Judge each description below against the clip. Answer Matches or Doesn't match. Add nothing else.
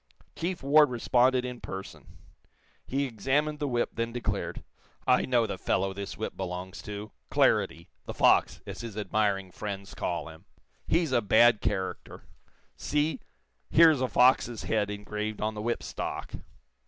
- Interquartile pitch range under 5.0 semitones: Matches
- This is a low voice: Matches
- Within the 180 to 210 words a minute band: Doesn't match